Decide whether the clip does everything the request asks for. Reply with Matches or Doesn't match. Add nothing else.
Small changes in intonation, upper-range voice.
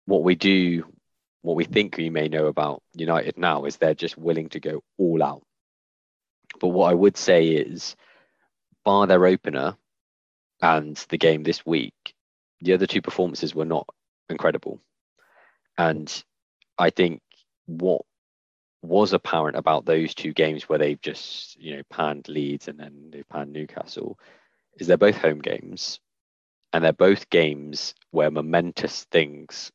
Doesn't match